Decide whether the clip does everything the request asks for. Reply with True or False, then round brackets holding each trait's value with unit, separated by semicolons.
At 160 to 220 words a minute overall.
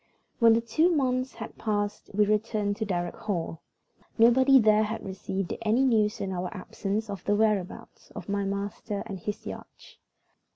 True (165 wpm)